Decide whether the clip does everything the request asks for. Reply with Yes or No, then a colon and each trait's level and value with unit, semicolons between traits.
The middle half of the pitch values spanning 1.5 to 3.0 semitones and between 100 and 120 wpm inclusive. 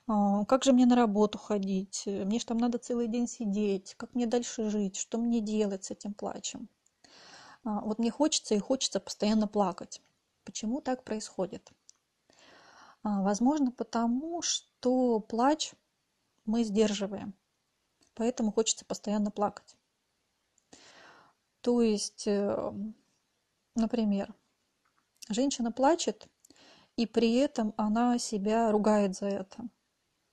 Yes: narrow, 2.5 semitones; slow, 110 wpm